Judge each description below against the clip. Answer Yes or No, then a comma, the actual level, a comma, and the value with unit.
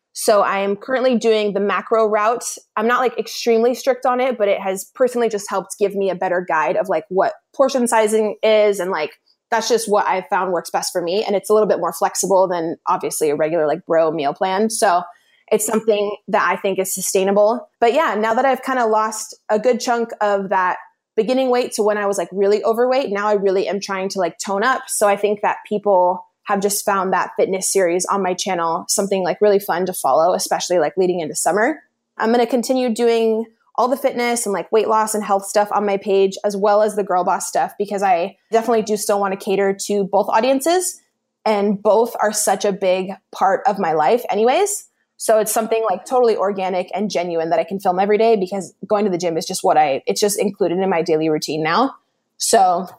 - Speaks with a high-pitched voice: Yes, high, 205 Hz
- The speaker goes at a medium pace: No, fast, 225 wpm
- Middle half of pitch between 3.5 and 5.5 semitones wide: No, average, 3.0 semitones